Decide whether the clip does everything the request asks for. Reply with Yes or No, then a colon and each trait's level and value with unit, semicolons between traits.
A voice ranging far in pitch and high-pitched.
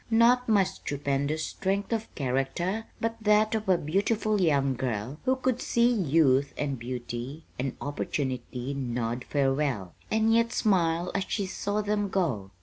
No: wide, 7.9 semitones; medium, 165 Hz